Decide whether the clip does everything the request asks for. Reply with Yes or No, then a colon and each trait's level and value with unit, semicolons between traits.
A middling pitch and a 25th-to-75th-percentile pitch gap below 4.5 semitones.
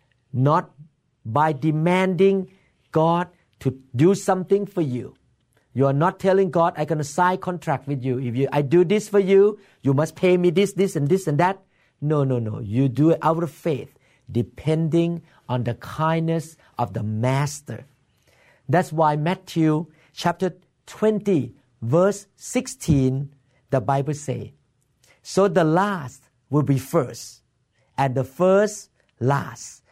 No: medium, 155 Hz; average, 5.2 semitones